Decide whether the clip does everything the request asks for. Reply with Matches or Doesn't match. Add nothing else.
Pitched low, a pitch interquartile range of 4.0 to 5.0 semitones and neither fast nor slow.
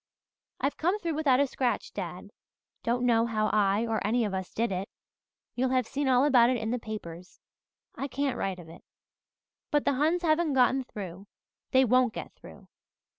Doesn't match